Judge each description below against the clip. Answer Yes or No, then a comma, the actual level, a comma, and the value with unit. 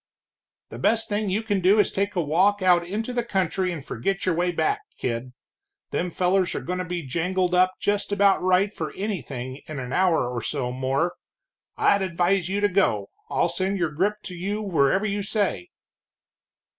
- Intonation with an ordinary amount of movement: Yes, average, 3.4 semitones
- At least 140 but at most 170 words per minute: No, average, 195 wpm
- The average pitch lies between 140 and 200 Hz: Yes, medium, 185 Hz